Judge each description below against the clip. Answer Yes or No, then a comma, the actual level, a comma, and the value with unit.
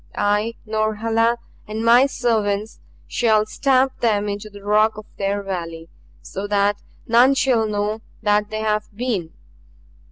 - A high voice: Yes, high, 215 Hz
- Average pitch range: No, narrow, 2.0 semitones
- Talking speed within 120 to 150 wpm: Yes, slow, 135 wpm